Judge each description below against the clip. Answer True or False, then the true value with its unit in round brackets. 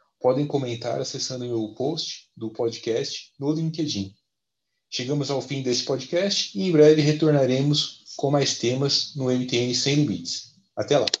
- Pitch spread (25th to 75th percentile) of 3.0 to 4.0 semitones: True (3.4 semitones)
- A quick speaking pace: False (150 wpm)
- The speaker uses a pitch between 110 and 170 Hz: True (140 Hz)